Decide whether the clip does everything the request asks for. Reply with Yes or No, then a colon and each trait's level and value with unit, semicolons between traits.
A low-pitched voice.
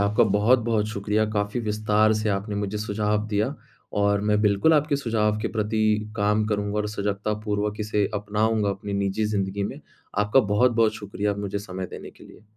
Yes: low, 105 Hz